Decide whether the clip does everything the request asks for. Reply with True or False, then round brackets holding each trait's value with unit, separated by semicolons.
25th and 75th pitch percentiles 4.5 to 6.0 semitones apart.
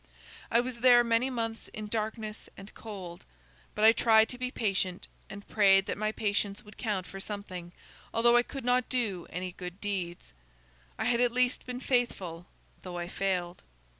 False (3.9 semitones)